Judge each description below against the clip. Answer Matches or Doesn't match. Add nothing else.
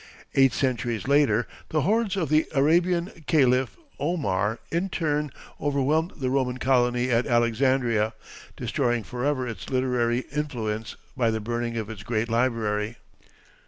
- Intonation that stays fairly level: Doesn't match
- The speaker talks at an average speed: Doesn't match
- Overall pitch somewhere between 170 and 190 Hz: Doesn't match